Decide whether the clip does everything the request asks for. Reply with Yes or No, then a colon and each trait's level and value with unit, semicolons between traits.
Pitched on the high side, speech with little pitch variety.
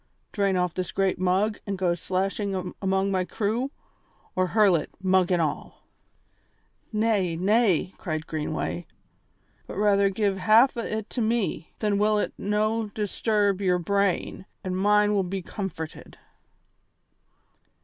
Yes: high, 195 Hz; narrow, 2.3 semitones